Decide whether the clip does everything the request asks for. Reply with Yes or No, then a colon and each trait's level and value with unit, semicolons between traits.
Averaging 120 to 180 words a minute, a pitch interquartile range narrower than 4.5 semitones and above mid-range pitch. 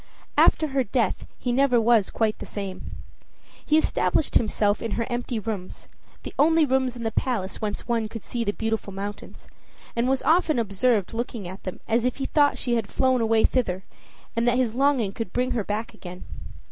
No: average, 195 wpm; average, 3.4 semitones; high, 230 Hz